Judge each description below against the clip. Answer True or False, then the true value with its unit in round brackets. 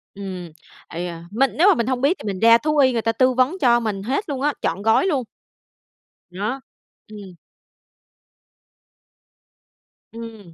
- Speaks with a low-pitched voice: False (230 Hz)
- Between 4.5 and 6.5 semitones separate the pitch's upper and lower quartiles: True (5.0 semitones)